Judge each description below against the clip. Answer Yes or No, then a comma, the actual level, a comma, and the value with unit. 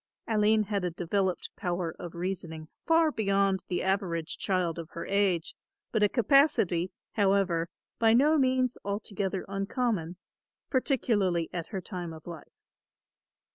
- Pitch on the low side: No, high, 195 Hz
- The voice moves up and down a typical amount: Yes, average, 3.9 semitones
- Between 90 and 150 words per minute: Yes, slow, 135 wpm